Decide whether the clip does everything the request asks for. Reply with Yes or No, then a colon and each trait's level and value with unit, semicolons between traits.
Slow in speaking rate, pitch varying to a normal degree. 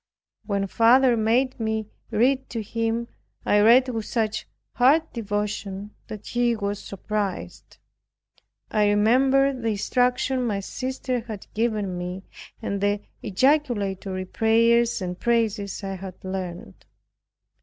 Yes: slow, 120 wpm; average, 3.3 semitones